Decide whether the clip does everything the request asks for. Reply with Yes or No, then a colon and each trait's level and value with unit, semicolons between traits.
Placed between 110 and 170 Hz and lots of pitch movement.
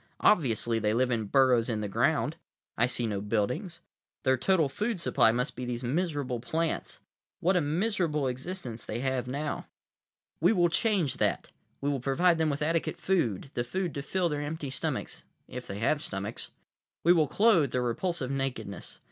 Yes: low, 135 Hz; wide, 5.7 semitones